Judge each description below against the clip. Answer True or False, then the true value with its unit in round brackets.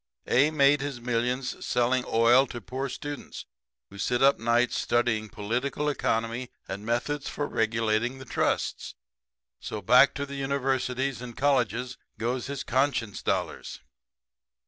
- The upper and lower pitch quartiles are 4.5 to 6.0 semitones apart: False (2.9 semitones)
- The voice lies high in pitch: False (125 Hz)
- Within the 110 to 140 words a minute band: True (135 wpm)